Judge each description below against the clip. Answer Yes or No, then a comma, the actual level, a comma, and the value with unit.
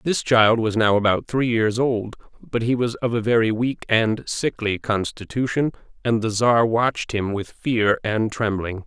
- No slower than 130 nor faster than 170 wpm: No, average, 185 wpm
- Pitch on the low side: Yes, low, 115 Hz